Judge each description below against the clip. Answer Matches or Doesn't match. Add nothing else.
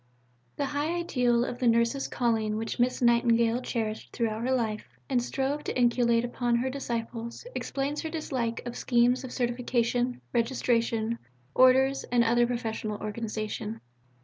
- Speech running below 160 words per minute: Matches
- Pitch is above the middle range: Matches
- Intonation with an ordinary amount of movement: Doesn't match